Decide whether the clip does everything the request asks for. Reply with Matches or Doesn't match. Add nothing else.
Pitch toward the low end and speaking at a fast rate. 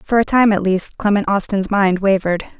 Doesn't match